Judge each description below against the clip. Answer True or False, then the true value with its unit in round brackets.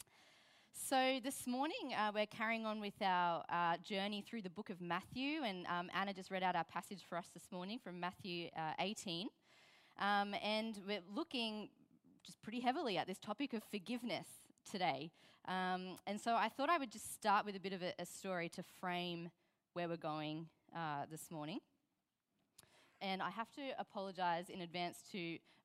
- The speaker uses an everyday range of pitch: True (3.9 semitones)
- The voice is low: False (195 Hz)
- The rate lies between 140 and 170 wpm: False (180 wpm)